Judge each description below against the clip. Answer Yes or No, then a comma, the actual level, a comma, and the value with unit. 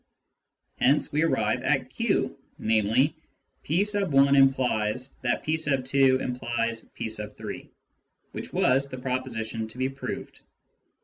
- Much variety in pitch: No, average, 3.2 semitones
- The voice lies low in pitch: Yes, low, 130 Hz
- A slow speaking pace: Yes, slow, 130 wpm